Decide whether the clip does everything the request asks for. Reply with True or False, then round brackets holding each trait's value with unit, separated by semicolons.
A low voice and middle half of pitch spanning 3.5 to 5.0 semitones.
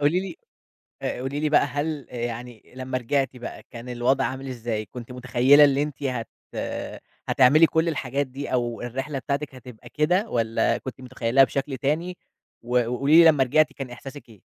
False (130 Hz; 2.9 semitones)